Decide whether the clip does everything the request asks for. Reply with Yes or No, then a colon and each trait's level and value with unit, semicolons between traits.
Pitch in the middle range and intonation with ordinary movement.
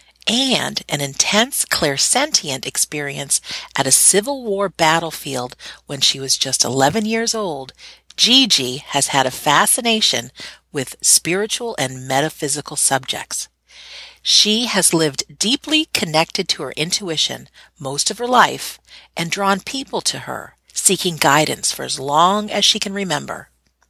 No: medium, 175 Hz; wide, 7.4 semitones